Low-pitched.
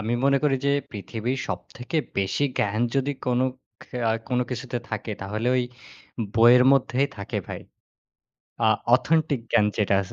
Yes: low, 125 Hz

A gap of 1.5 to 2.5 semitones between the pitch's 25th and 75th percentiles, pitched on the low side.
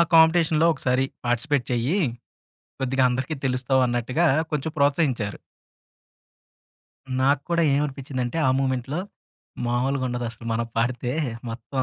No: average, 2.9 semitones; low, 130 Hz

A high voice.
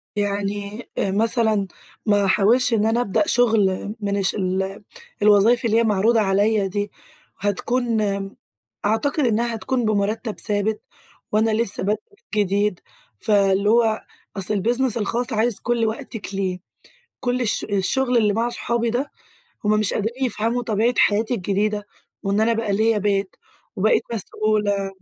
Yes: high, 215 Hz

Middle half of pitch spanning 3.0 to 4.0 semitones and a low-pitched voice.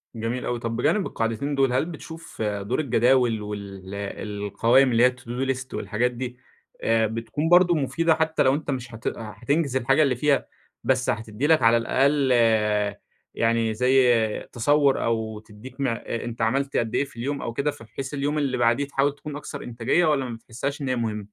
Yes: average, 3.5 semitones; low, 125 Hz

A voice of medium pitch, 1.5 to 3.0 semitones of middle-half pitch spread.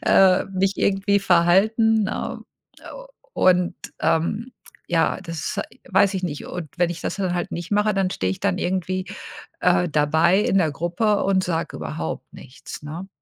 Yes: medium, 180 Hz; average, 2.7 semitones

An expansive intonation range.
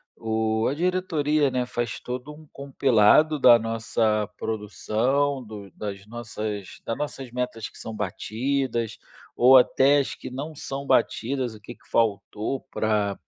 No: average, 4.2 semitones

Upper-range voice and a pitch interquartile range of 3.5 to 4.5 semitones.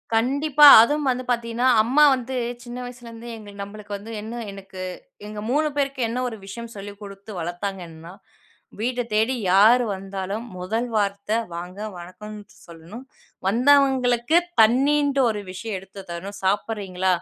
Yes: high, 220 Hz; average, 4.1 semitones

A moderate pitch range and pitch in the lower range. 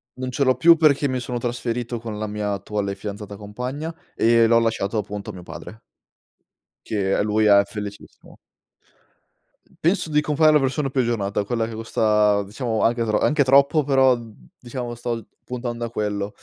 Yes: average, 3.7 semitones; low, 115 Hz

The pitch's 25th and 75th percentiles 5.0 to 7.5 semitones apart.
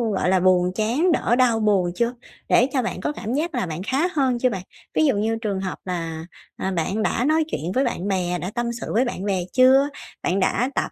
Yes: wide, 5.5 semitones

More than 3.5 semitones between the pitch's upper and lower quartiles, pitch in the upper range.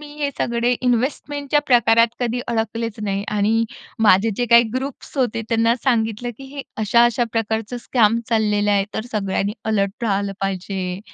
No: average, 2.7 semitones; high, 225 Hz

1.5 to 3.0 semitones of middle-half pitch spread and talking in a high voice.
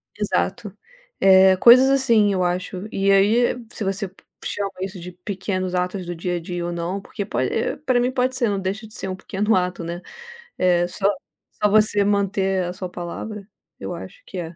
Yes: narrow, 2.6 semitones; high, 195 Hz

